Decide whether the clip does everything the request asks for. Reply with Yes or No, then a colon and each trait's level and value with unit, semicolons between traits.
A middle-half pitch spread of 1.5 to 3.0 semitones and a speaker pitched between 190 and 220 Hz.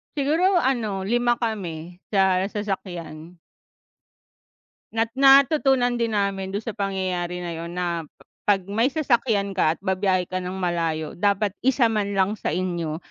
No: average, 4.3 semitones; high, 195 Hz